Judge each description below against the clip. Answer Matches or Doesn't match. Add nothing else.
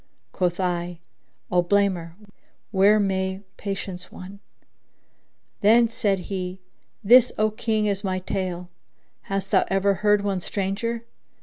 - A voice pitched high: Matches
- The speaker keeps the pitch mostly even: Matches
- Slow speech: Matches